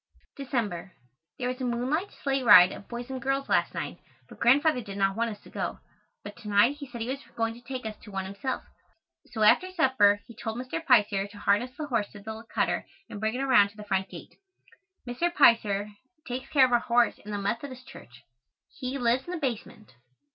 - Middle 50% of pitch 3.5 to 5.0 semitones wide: Yes, average, 4.1 semitones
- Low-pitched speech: No, high, 235 Hz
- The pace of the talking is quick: Yes, fast, 215 wpm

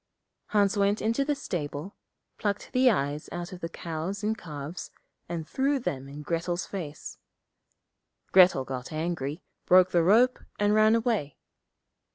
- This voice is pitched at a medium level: Yes, medium, 180 Hz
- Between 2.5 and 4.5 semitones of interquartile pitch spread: No, wide, 5.5 semitones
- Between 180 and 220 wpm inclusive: No, average, 145 wpm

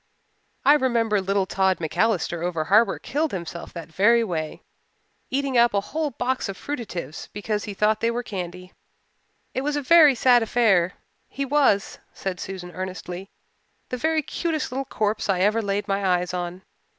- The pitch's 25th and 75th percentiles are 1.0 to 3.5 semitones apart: No, wide, 5.6 semitones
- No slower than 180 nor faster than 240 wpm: No, average, 165 wpm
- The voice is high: Yes, high, 205 Hz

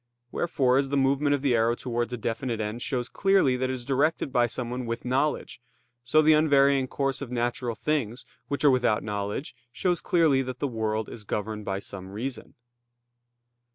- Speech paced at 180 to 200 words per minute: Yes, average, 185 wpm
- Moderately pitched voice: No, low, 125 Hz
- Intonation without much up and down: No, average, 3.2 semitones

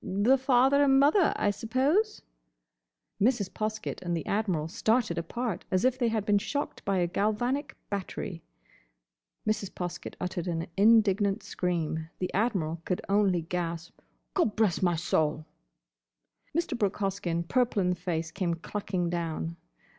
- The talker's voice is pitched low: No, high, 195 Hz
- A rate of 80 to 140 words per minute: Yes, slow, 135 wpm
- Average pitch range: Yes, average, 4.7 semitones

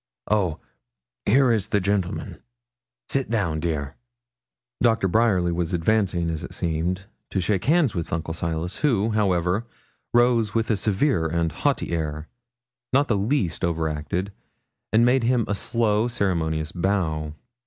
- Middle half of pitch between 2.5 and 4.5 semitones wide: No, average, 5.3 semitones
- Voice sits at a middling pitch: No, very low, 95 Hz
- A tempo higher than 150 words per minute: No, average, 145 wpm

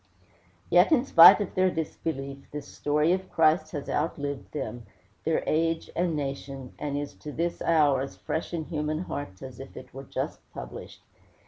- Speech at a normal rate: Yes, average, 175 wpm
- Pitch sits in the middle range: Yes, medium, 150 Hz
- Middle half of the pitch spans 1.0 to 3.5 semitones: Yes, average, 3.2 semitones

